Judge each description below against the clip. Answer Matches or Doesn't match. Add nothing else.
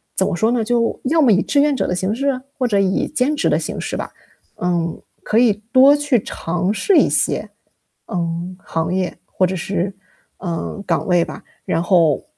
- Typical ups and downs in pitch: Doesn't match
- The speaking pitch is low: Doesn't match